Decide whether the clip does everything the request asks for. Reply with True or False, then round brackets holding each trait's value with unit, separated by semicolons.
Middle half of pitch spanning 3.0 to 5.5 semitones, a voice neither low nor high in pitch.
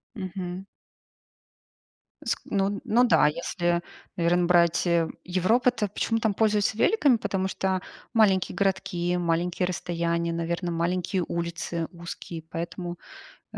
False (2.5 semitones; 180 Hz)